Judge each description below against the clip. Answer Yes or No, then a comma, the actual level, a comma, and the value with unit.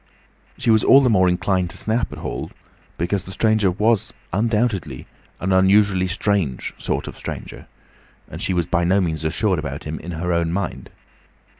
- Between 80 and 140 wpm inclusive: No, average, 175 wpm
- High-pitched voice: No, very low, 95 Hz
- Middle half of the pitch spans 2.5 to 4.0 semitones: Yes, average, 3.5 semitones